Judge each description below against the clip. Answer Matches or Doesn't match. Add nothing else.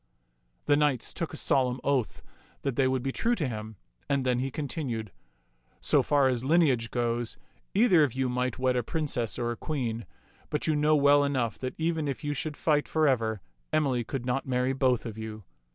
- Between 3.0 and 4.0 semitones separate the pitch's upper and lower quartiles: Matches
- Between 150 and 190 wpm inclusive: Doesn't match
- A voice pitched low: Matches